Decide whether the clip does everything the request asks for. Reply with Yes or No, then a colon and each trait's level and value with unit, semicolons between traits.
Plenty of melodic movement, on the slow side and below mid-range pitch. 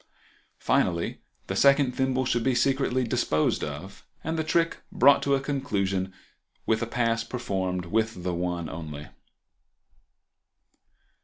Yes: wide, 6.5 semitones; slow, 130 wpm; low, 115 Hz